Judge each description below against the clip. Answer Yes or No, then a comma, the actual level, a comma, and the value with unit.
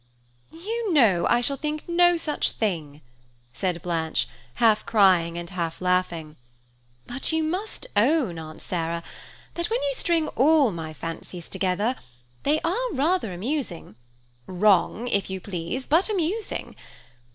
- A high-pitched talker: Yes, high, 210 Hz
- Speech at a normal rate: No, slow, 130 wpm